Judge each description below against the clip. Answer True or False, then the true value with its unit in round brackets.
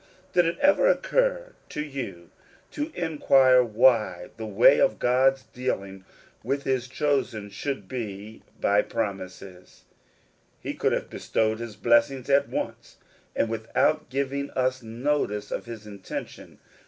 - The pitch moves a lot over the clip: False (4.7 semitones)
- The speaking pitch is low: True (120 Hz)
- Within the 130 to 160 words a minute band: True (135 wpm)